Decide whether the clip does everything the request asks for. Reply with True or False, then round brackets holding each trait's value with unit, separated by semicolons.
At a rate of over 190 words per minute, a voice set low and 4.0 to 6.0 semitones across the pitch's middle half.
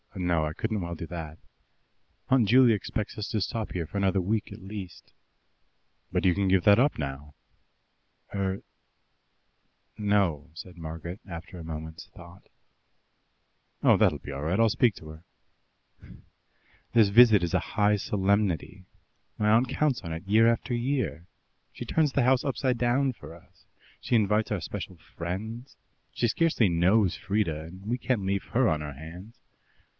False (160 wpm; 100 Hz; 5.0 semitones)